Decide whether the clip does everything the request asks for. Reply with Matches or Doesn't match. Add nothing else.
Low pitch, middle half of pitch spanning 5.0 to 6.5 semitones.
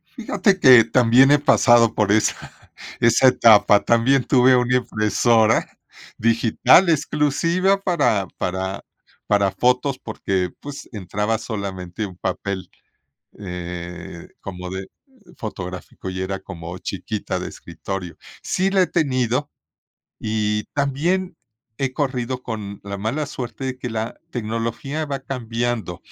Matches